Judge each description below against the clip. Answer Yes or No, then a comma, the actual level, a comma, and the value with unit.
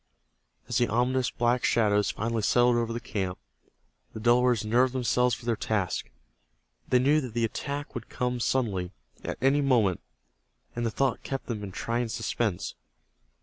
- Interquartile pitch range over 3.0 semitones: No, narrow, 2.4 semitones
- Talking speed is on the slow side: No, average, 160 wpm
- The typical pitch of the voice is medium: No, low, 120 Hz